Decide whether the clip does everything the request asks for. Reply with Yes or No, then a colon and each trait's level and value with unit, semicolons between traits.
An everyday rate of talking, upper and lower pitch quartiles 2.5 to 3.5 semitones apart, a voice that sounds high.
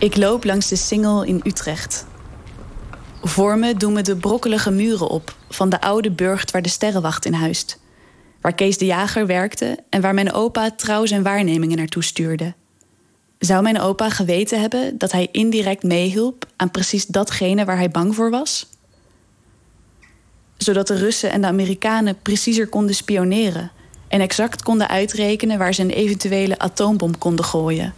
Yes: average, 160 wpm; average, 3.1 semitones; high, 195 Hz